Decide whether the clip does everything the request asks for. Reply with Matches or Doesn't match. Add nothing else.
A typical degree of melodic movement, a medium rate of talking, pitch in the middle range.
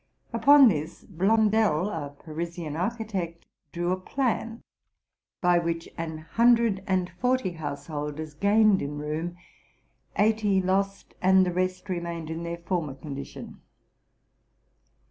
Doesn't match